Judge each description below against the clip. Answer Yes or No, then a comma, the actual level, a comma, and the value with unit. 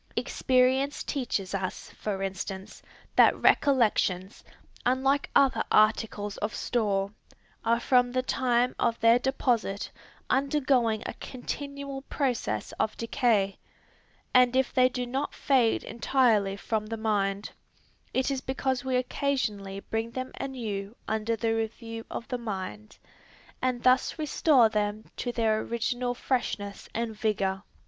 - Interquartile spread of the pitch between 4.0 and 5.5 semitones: No, average, 3.5 semitones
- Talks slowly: Yes, slow, 125 wpm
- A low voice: No, high, 235 Hz